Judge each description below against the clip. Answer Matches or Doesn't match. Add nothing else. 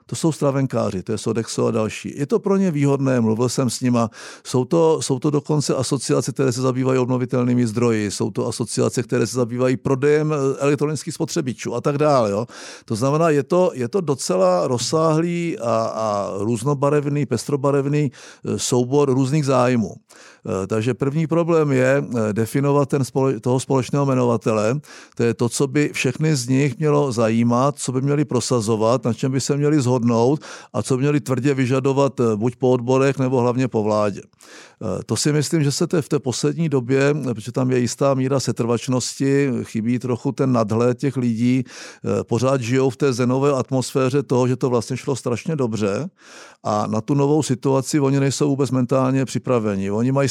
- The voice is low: Matches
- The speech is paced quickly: Matches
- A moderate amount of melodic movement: Matches